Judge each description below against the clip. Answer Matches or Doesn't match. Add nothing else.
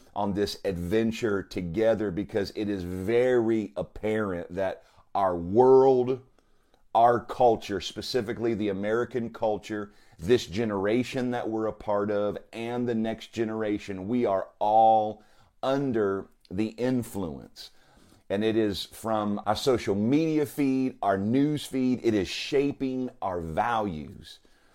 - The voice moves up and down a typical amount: Matches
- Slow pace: Matches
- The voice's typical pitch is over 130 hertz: Doesn't match